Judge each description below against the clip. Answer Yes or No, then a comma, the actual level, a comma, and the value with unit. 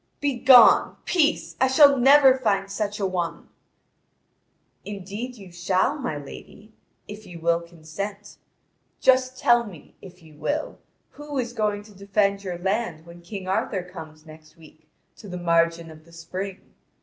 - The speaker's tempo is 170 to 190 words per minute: No, average, 150 wpm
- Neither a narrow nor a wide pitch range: No, wide, 5.7 semitones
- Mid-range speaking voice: No, high, 195 Hz